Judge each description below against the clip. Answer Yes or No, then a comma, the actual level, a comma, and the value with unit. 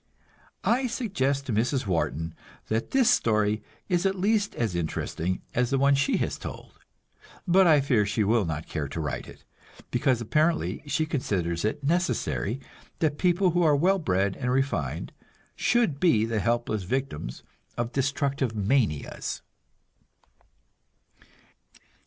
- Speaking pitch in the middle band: No, low, 130 Hz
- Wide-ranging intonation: Yes, wide, 7.1 semitones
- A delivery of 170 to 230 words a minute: No, average, 140 wpm